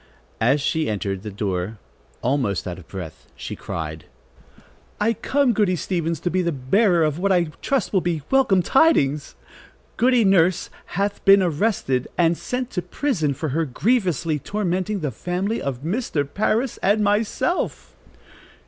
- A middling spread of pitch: No, wide, 7.1 semitones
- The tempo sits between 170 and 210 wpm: No, average, 150 wpm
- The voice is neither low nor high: Yes, medium, 175 Hz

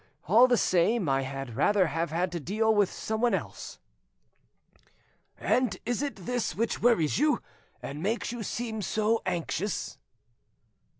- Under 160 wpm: Yes, average, 140 wpm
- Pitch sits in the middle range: No, high, 210 Hz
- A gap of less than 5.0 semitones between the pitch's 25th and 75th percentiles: No, wide, 5.5 semitones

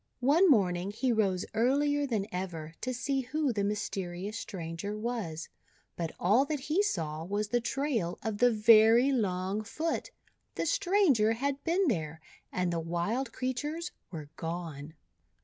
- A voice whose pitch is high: Yes, high, 220 Hz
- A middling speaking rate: Yes, average, 150 wpm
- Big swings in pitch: Yes, wide, 7.0 semitones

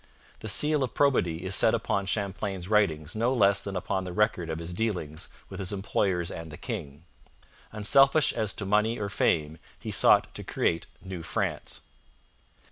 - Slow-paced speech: No, average, 170 wpm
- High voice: No, very low, 95 Hz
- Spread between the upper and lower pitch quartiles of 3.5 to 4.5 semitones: Yes, average, 3.8 semitones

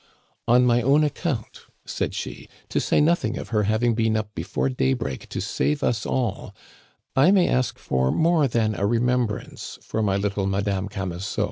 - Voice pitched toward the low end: Yes, low, 115 Hz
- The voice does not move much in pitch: No, average, 4.4 semitones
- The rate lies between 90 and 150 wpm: No, average, 170 wpm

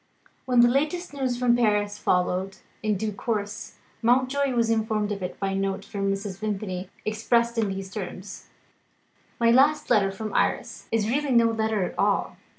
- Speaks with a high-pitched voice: Yes, high, 215 Hz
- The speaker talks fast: No, average, 170 wpm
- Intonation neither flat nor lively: Yes, average, 3.4 semitones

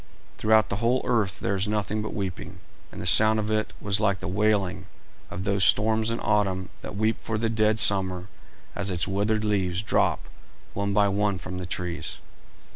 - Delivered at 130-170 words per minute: No, average, 190 wpm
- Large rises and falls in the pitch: No, narrow, 2.4 semitones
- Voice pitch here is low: Yes, low, 100 Hz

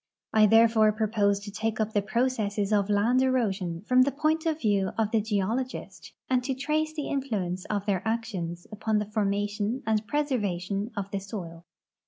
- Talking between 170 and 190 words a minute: Yes, average, 175 wpm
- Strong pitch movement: No, average, 3.8 semitones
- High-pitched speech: Yes, high, 215 Hz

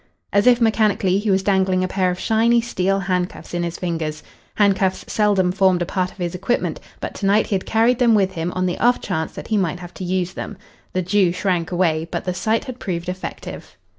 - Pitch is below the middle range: No, medium, 185 Hz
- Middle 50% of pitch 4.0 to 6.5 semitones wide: No, narrow, 2.5 semitones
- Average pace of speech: No, fast, 225 wpm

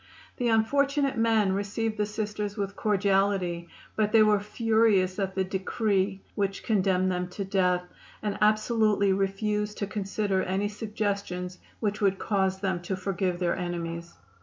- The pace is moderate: Yes, average, 145 wpm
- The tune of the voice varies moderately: No, narrow, 2.1 semitones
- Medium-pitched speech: No, high, 200 Hz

